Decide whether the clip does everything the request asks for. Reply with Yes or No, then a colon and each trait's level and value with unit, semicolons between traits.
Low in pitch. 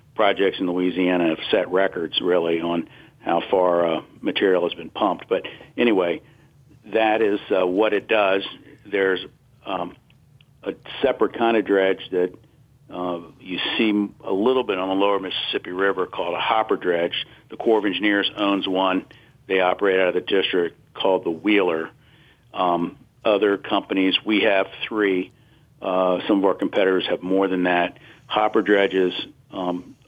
Yes: very low, 95 Hz